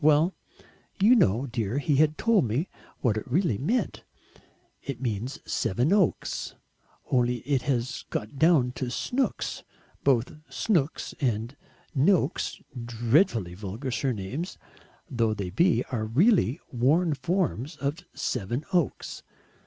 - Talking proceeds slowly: Yes, slow, 115 wpm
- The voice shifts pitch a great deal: Yes, wide, 5.8 semitones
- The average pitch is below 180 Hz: Yes, low, 135 Hz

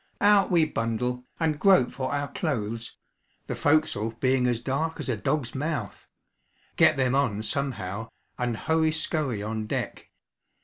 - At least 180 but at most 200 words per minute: No, average, 145 wpm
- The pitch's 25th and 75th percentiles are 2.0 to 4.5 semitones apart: No, average, 5.3 semitones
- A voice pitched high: No, low, 130 Hz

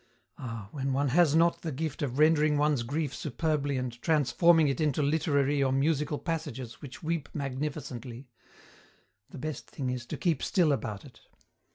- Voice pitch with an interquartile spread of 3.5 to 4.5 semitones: No, average, 3.1 semitones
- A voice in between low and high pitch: Yes, medium, 145 Hz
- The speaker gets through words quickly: No, average, 165 wpm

